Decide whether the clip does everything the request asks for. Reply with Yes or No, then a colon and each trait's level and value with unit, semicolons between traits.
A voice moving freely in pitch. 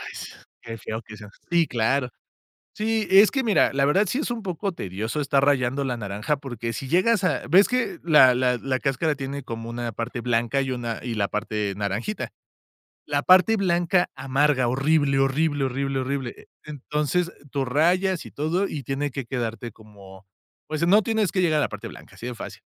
Yes: wide, 6.2 semitones